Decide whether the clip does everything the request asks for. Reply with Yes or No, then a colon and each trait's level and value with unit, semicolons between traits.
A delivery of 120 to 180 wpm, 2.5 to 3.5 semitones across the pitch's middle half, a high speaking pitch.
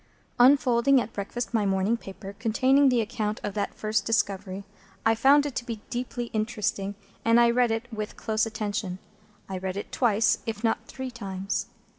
Yes: average, 175 wpm; average, 2.9 semitones; high, 225 Hz